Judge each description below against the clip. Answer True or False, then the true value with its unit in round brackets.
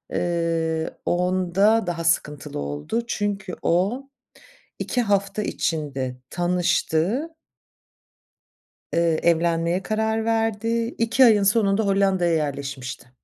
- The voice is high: False (180 Hz)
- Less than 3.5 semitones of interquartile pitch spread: False (4.7 semitones)